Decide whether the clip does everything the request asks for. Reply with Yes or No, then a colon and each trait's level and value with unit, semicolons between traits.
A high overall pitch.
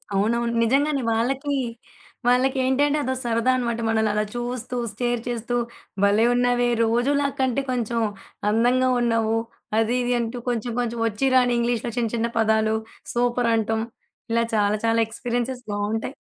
Yes: high, 240 Hz